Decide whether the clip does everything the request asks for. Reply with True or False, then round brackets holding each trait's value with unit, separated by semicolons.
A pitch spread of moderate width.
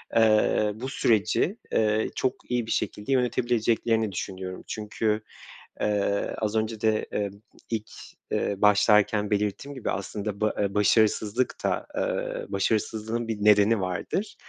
False (1.6 semitones)